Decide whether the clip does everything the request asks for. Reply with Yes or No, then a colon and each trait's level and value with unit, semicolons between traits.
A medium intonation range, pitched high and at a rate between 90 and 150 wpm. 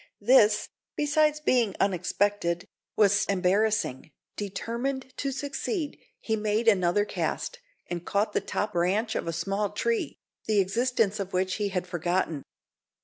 Yes: average, 3.9 semitones; high, 205 Hz; slow, 135 wpm